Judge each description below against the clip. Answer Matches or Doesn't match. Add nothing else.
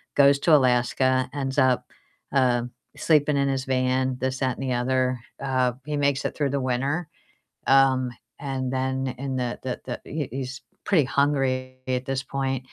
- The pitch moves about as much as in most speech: Doesn't match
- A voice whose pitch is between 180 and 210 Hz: Doesn't match